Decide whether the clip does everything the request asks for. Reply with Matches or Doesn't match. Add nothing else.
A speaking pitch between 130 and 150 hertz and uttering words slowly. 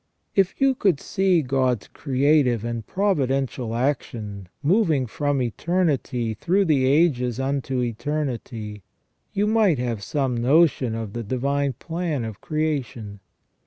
Matches